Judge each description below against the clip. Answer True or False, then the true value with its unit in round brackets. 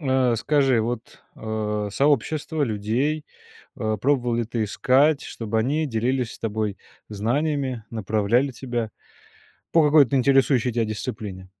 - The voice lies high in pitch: False (120 Hz)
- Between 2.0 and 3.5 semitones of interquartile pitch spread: False (4.1 semitones)